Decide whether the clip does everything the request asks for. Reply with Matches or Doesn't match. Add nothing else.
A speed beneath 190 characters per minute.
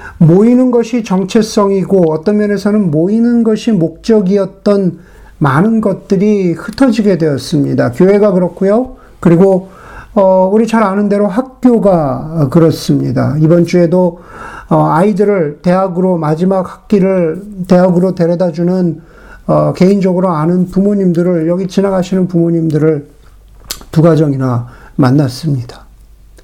Doesn't match